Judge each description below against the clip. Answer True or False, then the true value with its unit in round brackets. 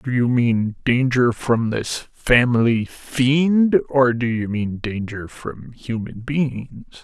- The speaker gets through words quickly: False (135 wpm)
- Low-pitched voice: True (120 Hz)